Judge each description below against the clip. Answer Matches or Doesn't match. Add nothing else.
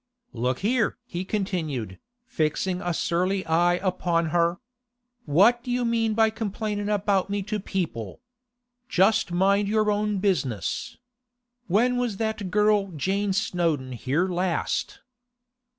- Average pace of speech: Doesn't match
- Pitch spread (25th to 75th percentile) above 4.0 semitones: Doesn't match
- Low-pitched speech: Doesn't match